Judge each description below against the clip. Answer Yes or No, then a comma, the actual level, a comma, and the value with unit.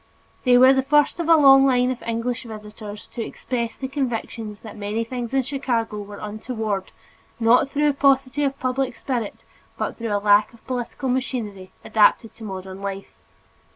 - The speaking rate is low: No, average, 175 wpm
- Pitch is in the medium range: No, high, 235 Hz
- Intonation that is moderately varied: Yes, average, 3.8 semitones